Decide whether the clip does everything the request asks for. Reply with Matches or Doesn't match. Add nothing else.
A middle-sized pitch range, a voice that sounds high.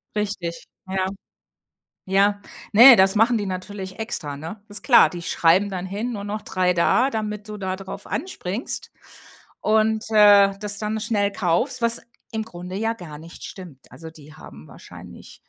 Matches